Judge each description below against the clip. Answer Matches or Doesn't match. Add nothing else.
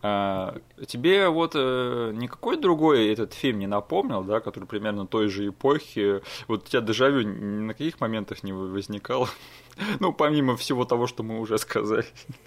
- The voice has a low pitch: Matches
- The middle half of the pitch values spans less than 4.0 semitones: Doesn't match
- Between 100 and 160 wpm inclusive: Doesn't match